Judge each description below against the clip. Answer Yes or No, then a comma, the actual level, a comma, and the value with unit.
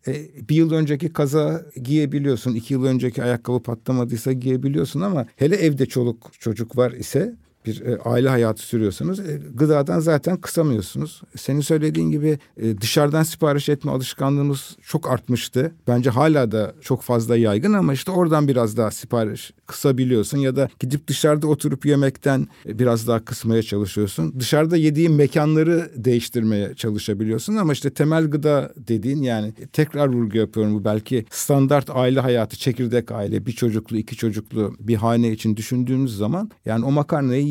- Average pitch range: Yes, average, 4.4 semitones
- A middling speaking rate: No, fast, 145 wpm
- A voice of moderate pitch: No, low, 130 Hz